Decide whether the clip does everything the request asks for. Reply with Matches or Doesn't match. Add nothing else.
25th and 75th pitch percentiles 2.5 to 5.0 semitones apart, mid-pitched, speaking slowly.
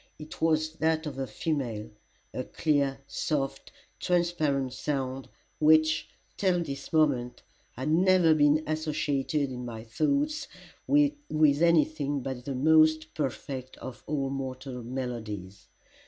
Matches